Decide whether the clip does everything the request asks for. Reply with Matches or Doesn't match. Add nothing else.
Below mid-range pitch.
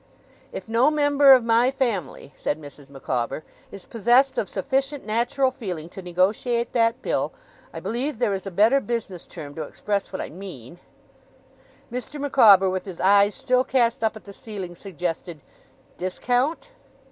Doesn't match